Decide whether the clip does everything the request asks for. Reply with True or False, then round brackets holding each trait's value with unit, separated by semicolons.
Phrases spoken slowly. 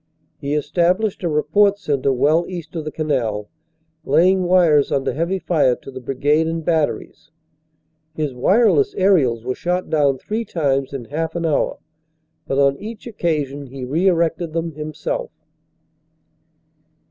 False (145 wpm)